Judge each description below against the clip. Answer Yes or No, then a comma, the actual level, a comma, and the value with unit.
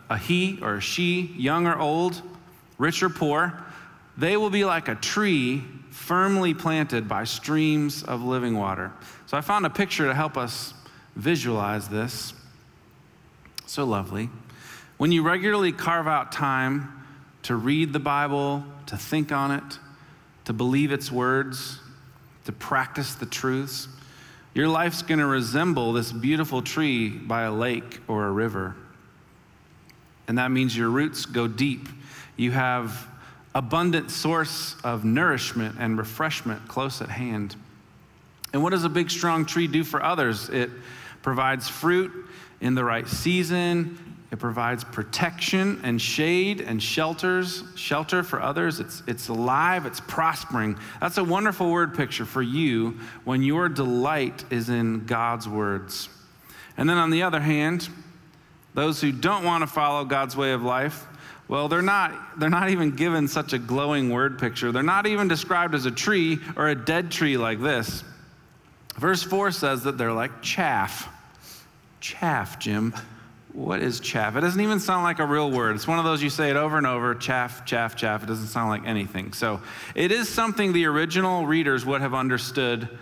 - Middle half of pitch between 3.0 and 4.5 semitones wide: No, average, 5.3 semitones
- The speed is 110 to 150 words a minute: No, average, 165 wpm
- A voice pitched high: No, medium, 140 Hz